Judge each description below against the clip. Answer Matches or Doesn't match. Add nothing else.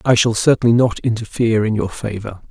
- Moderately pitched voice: Doesn't match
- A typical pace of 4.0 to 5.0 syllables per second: Doesn't match